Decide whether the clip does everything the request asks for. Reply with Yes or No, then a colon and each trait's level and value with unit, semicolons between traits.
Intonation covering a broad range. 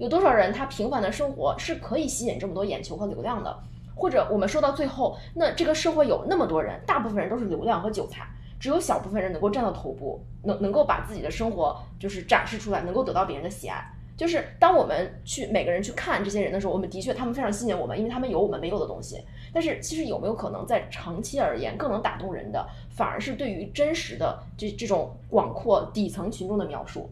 Yes: wide, 7.3 semitones